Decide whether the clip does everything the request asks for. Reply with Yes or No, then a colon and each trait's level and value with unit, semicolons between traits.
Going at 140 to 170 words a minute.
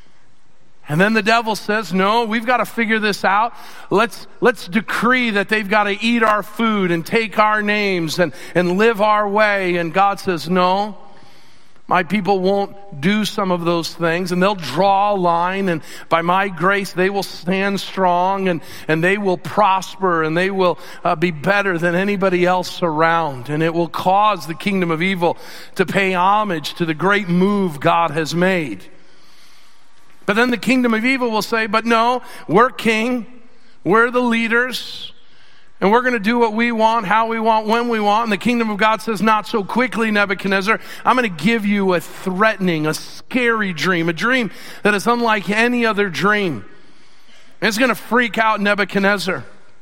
No: average, 185 wpm